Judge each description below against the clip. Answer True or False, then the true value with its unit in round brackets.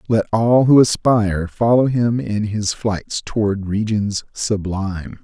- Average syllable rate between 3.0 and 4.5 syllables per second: True (3.9 syllables/s)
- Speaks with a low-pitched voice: True (105 Hz)